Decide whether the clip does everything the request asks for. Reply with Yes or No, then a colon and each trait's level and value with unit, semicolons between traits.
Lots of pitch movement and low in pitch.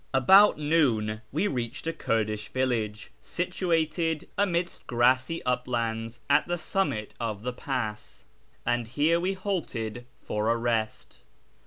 Yes: wide, 6.6 semitones; low, 125 Hz